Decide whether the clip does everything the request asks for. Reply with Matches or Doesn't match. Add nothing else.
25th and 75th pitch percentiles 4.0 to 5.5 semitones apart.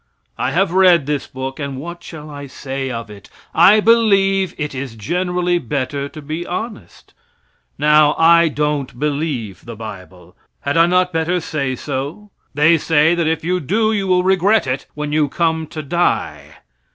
Matches